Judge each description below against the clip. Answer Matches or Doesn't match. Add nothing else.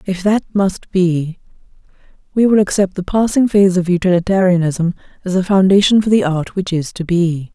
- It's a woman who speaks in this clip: Matches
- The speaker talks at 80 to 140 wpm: Doesn't match